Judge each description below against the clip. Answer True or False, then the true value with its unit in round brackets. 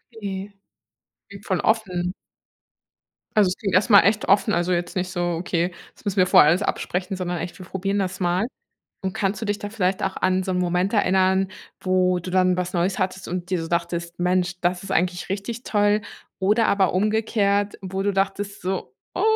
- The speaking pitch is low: False (185 Hz)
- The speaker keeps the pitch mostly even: True (1.9 semitones)